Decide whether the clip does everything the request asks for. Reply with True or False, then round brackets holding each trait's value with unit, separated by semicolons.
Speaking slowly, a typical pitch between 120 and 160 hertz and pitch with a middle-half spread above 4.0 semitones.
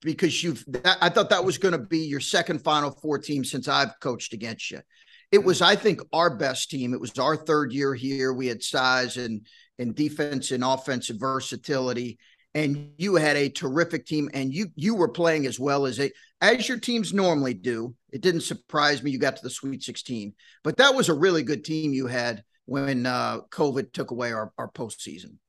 False (205 wpm; 140 Hz; 4.5 semitones)